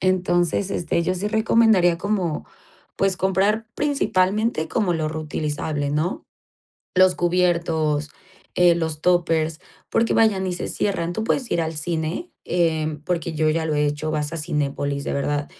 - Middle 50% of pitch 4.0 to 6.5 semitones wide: No, average, 3.2 semitones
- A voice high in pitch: No, medium, 170 Hz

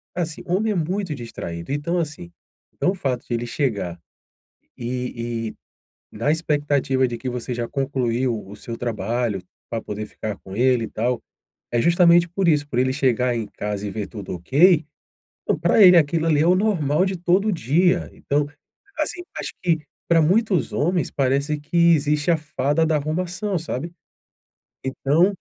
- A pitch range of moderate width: No, wide, 6.1 semitones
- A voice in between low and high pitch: Yes, medium, 145 Hz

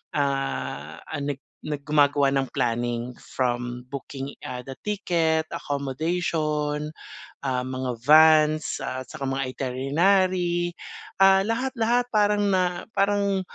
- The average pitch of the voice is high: No, medium, 150 Hz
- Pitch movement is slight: No, average, 5.2 semitones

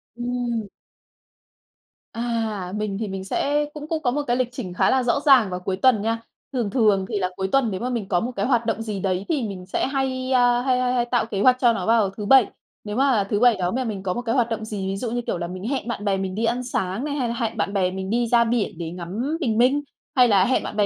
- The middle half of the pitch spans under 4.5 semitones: Yes, average, 4.1 semitones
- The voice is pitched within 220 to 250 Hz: Yes, high, 230 Hz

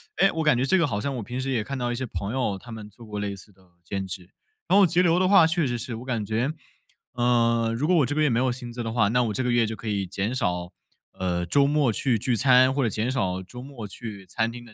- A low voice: Yes, low, 120 Hz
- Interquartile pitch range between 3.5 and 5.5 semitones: Yes, average, 4.1 semitones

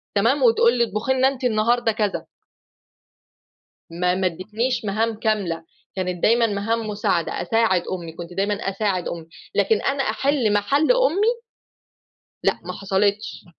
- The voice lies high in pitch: Yes, high, 215 Hz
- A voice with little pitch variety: No, average, 3.8 semitones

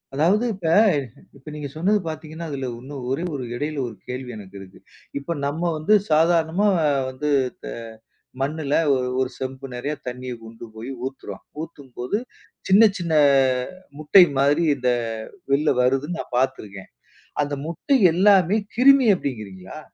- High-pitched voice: No, medium, 145 Hz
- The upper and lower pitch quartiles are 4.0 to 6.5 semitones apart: Yes, average, 4.8 semitones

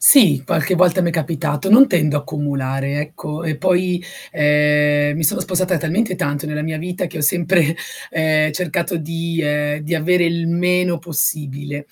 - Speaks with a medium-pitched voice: Yes, medium, 160 Hz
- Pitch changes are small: No, average, 3.1 semitones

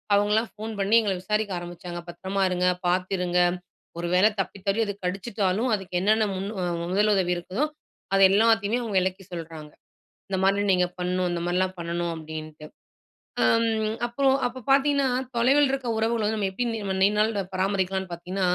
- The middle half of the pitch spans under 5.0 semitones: Yes, average, 3.5 semitones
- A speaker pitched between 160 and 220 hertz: Yes, high, 195 Hz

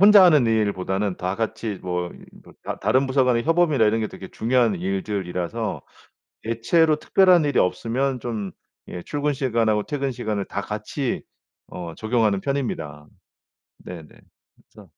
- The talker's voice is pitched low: Yes, low, 115 Hz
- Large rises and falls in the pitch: Yes, wide, 5.7 semitones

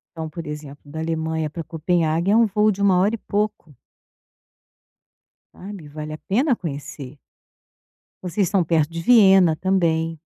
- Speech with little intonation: No, average, 3.8 semitones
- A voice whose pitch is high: No, medium, 165 Hz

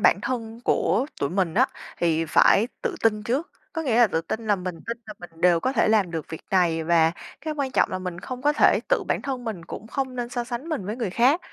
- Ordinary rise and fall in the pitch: No, wide, 6.4 semitones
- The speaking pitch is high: Yes, high, 220 Hz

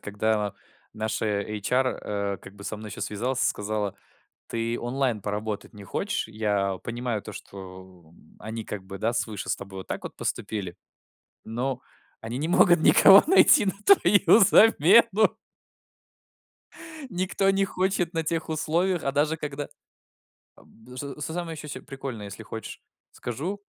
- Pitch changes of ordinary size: No, wide, 7.7 semitones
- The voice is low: Yes, low, 120 Hz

